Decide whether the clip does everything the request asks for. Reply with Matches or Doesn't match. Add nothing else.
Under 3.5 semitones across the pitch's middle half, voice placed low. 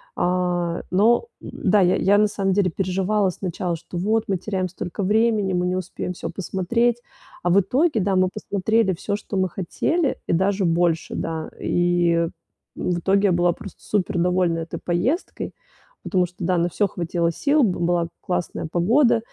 Doesn't match